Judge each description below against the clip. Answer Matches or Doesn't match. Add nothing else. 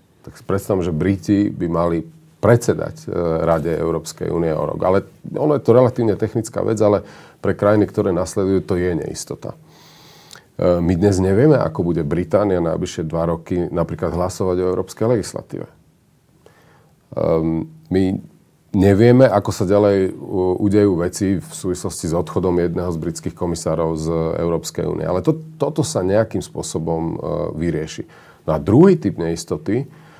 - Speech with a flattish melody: Doesn't match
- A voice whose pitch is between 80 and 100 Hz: Matches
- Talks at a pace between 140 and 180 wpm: Matches